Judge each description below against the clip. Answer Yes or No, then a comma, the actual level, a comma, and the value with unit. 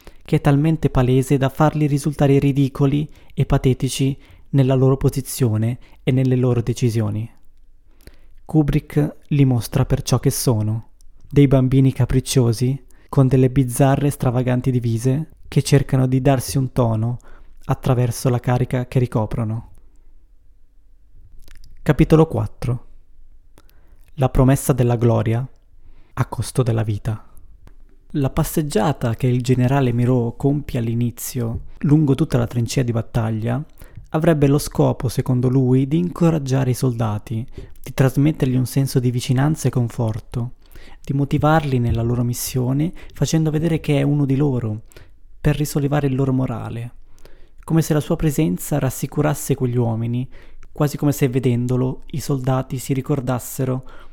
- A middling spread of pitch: Yes, average, 3.5 semitones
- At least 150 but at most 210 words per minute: No, average, 130 wpm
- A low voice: Yes, low, 130 Hz